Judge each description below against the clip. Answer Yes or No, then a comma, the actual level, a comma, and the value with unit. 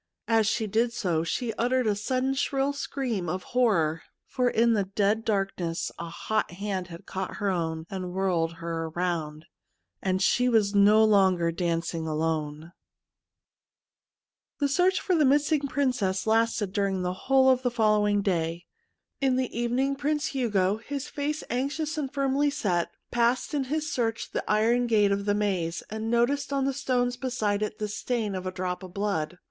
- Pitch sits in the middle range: No, high, 215 Hz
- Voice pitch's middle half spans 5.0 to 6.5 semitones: Yes, wide, 5.6 semitones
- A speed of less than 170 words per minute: No, average, 175 wpm